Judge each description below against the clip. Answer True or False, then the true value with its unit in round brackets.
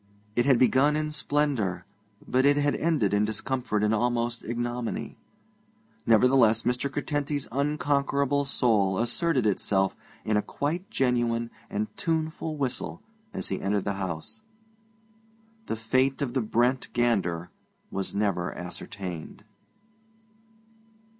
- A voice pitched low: True (120 Hz)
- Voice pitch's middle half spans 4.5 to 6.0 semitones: True (5.1 semitones)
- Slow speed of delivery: True (120 wpm)